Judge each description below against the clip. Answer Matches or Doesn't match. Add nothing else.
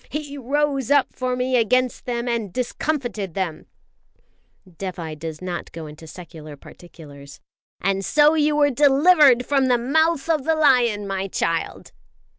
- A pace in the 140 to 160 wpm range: Matches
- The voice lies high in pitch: Matches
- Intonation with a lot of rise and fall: Matches